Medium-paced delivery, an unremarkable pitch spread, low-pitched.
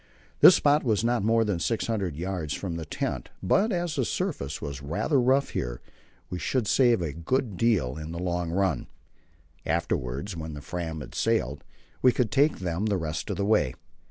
No: average, 185 wpm; wide, 6.6 semitones; very low, 95 Hz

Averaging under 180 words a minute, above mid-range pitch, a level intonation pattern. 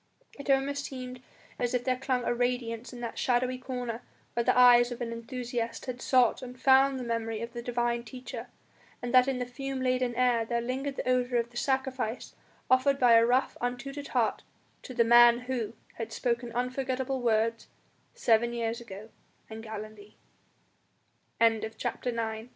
Yes: average, 170 wpm; high, 245 Hz; narrow, 1.6 semitones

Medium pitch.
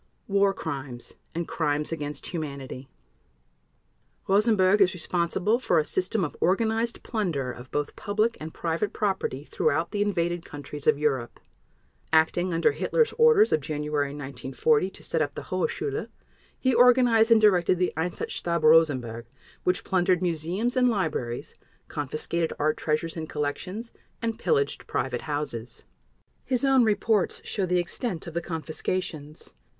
Yes: medium, 170 Hz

